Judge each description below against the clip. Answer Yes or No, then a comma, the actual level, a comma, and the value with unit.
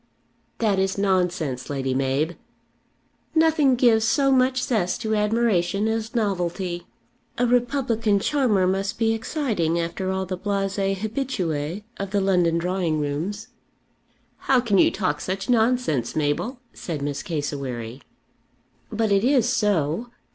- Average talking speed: No, slow, 130 wpm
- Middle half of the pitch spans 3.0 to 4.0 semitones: No, average, 5.1 semitones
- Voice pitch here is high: Yes, high, 195 Hz